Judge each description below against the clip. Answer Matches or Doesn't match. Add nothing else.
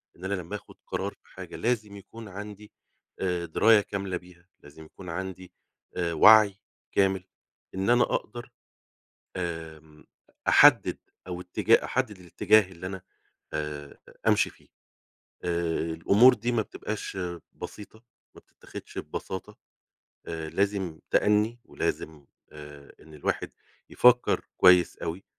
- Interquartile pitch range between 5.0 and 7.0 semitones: Doesn't match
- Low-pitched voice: Matches